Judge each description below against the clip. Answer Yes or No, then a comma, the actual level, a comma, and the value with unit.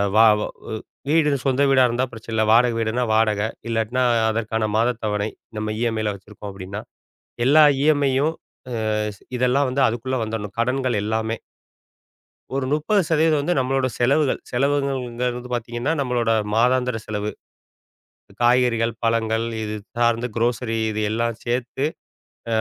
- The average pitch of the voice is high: No, low, 120 Hz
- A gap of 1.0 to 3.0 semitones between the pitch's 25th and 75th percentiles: Yes, average, 2.7 semitones